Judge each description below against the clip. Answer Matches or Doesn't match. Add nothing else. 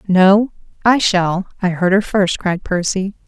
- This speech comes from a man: Doesn't match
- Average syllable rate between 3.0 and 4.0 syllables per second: Matches